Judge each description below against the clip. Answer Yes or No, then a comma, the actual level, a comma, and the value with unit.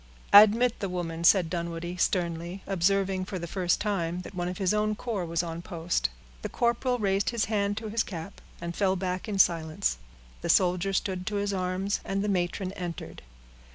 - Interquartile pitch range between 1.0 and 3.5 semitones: Yes, average, 2.7 semitones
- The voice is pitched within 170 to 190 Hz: Yes, medium, 185 Hz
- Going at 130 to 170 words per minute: No, average, 190 wpm